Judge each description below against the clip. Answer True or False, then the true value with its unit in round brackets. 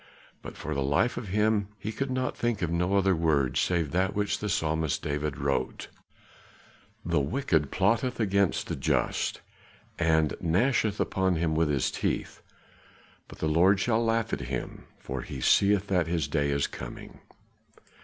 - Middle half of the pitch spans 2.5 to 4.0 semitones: False (5.1 semitones)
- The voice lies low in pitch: True (85 Hz)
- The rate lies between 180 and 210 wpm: False (160 wpm)